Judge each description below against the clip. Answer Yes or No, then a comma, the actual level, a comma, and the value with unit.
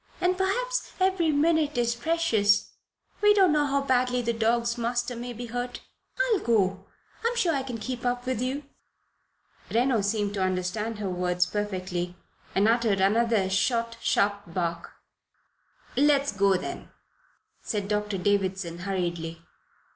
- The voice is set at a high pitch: Yes, high, 230 Hz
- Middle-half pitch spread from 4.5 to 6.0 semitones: Yes, average, 5.1 semitones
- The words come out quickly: No, average, 145 wpm